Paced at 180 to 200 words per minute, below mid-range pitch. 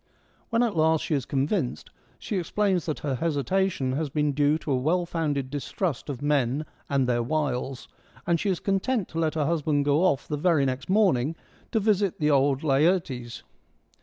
No: average, 185 wpm; medium, 150 Hz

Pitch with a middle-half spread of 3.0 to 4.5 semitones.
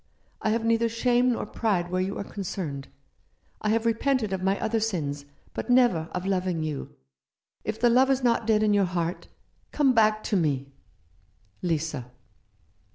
No: wide, 5.6 semitones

